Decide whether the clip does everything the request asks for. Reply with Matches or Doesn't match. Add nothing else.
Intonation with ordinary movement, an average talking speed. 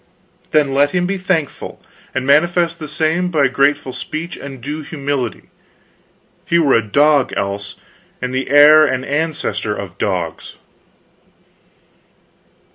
Doesn't match